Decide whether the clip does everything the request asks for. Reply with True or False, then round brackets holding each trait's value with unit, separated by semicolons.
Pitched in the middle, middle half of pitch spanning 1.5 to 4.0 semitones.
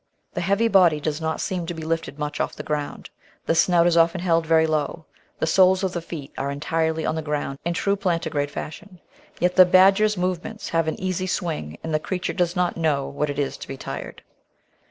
True (165 Hz; 3.0 semitones)